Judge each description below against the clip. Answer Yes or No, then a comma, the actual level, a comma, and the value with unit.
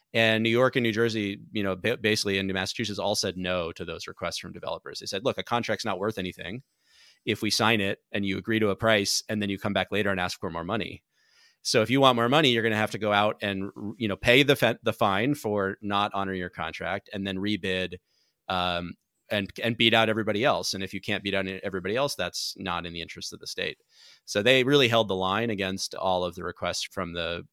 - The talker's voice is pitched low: Yes, low, 105 Hz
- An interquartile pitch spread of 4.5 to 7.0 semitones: No, average, 3.0 semitones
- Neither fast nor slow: No, fast, 245 wpm